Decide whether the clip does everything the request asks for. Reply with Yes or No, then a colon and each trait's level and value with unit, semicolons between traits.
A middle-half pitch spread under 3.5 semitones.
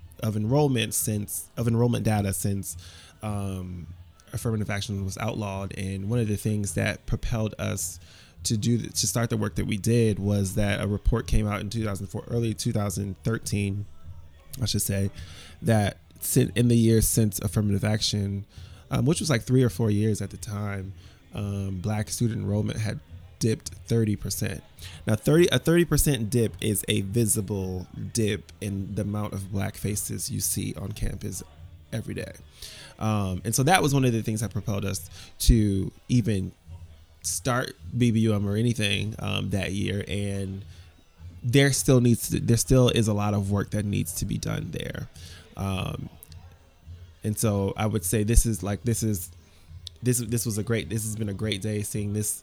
Yes: average, 2.9 semitones